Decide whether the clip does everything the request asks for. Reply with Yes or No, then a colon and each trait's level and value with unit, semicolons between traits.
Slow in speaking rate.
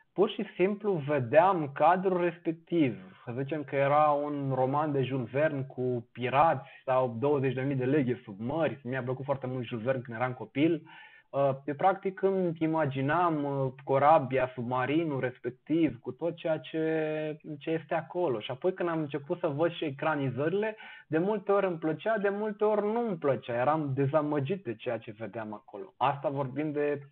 No: fast, 170 wpm